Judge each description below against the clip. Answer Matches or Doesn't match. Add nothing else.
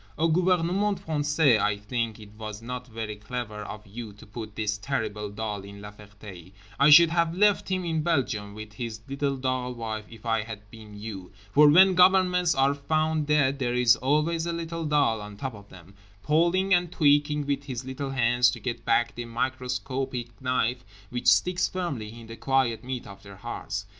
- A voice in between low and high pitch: Doesn't match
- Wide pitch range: Matches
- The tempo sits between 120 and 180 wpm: Doesn't match